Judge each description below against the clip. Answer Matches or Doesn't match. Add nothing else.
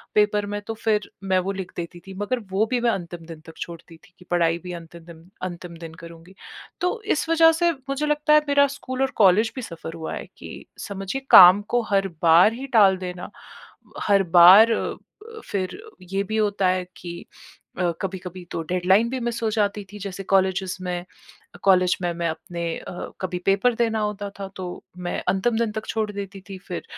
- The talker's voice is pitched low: Doesn't match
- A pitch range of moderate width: Matches